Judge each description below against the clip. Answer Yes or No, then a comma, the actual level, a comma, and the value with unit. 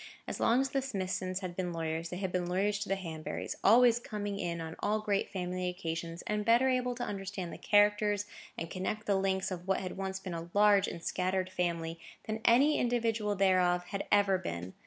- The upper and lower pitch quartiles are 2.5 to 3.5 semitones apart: Yes, average, 2.8 semitones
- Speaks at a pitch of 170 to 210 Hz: Yes, high, 190 Hz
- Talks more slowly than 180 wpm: No, fast, 205 wpm